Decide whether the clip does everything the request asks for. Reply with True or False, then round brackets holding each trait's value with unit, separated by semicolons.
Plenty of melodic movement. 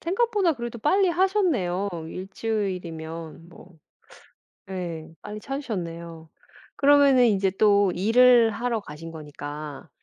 True (7.2 semitones)